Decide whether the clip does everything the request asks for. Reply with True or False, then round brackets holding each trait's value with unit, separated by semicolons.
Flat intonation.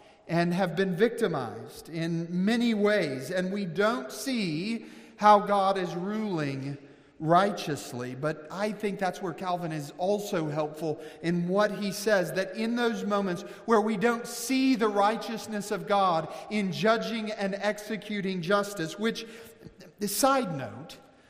False (4.0 semitones)